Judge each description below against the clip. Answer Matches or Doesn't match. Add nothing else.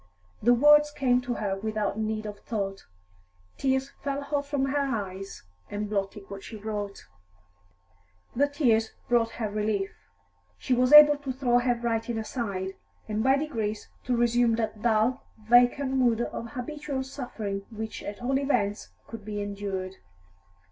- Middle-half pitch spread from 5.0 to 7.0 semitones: Doesn't match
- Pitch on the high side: Matches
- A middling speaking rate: Matches